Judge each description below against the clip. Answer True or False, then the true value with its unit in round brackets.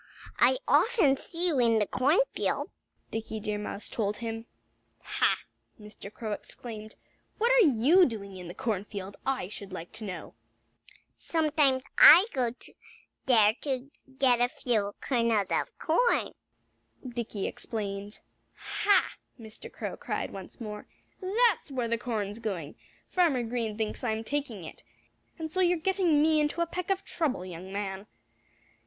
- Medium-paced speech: True (145 wpm)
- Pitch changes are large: True (6.6 semitones)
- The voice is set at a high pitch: True (235 Hz)